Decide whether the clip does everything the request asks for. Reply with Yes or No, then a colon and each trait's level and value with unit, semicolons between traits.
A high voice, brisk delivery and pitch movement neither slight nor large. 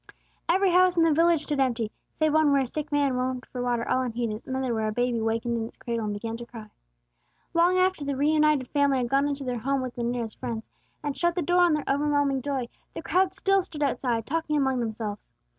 Yes: very high, 270 Hz; fast, 235 wpm; average, 4.3 semitones